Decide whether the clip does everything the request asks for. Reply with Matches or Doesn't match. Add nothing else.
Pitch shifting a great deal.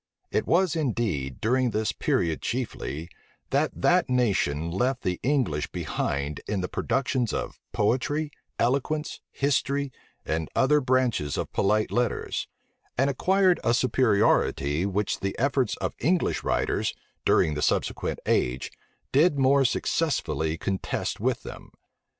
Matches